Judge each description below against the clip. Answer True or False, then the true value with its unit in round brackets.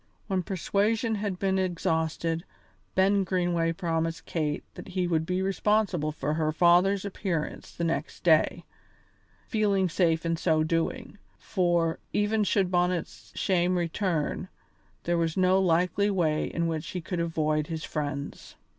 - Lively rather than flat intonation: False (2.7 semitones)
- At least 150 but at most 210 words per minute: False (140 wpm)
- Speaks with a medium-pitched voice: True (175 Hz)